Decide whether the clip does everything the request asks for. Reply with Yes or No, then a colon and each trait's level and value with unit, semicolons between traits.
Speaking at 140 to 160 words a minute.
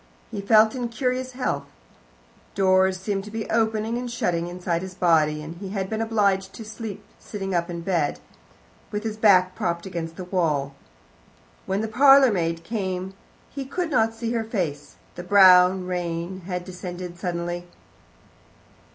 Yes: average, 155 wpm